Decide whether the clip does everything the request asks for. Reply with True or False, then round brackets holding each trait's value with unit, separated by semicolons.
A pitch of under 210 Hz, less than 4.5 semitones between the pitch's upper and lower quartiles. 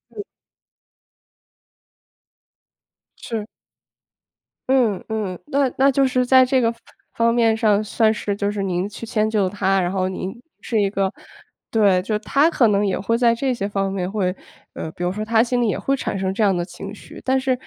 False (215 Hz; 3.7 semitones)